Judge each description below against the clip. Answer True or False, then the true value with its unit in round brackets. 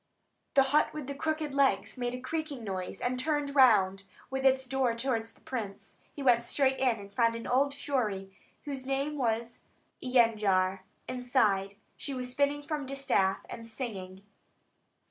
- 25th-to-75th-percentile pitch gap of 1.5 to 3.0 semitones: False (3.9 semitones)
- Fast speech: False (165 wpm)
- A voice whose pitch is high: True (250 Hz)